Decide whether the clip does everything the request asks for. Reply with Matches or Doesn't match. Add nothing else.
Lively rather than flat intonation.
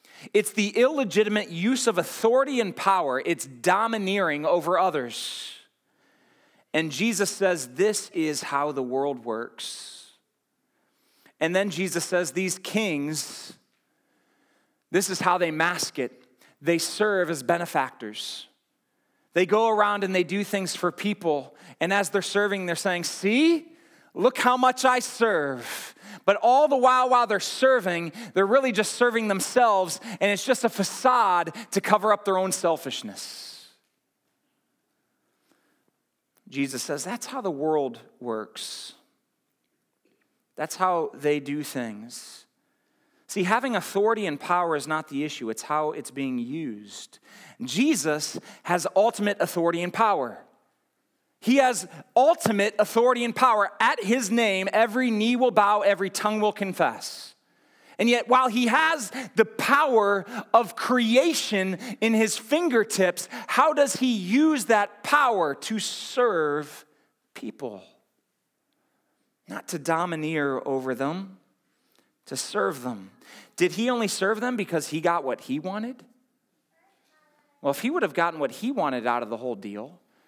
Matches